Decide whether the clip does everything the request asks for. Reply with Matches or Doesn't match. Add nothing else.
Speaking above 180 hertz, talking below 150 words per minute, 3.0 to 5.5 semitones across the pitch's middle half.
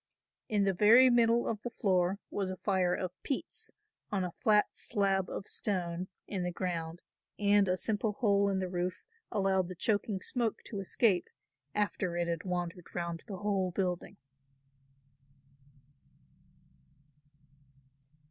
Doesn't match